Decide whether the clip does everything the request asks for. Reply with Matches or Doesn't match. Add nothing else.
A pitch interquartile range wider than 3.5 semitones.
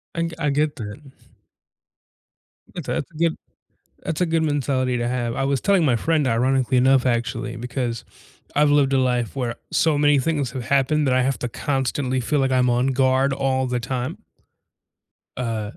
Doesn't match